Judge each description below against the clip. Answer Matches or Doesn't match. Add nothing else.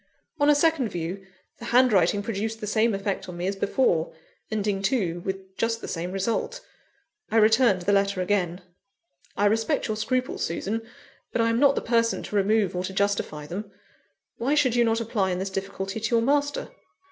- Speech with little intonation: Doesn't match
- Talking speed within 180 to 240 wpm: Matches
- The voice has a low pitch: Doesn't match